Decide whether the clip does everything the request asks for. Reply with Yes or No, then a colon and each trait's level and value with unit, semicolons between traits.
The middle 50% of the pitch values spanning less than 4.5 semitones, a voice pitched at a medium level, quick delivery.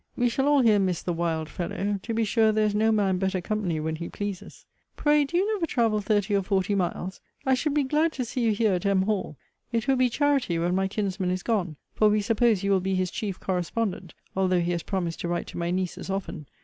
No: average, 4.0 semitones; high, 200 Hz; fast, 245 wpm